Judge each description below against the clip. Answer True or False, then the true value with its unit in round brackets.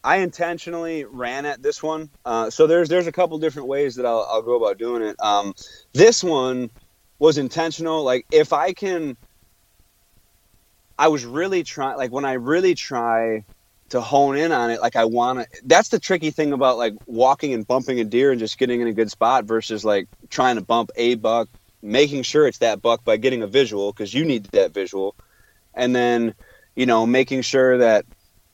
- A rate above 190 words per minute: True (200 wpm)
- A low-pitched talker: True (125 Hz)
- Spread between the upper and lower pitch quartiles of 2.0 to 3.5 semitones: False (5.1 semitones)